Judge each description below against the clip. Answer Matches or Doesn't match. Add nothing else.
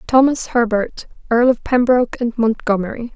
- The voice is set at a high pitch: Matches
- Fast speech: Doesn't match